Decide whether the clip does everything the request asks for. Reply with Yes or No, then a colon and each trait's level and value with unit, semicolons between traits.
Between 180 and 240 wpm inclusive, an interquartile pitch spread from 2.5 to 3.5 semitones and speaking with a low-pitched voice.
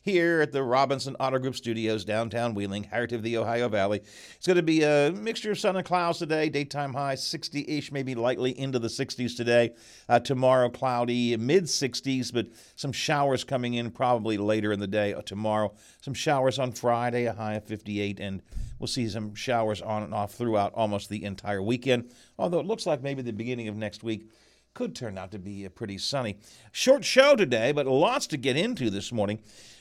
No: average, 200 wpm; average, 4.3 semitones; low, 120 Hz